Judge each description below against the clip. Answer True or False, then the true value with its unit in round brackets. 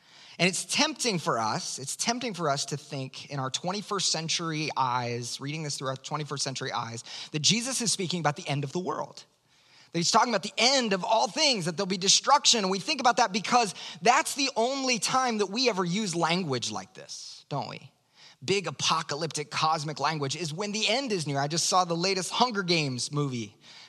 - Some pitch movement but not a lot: False (6.9 semitones)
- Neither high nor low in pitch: True (175 Hz)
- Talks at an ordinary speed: False (210 wpm)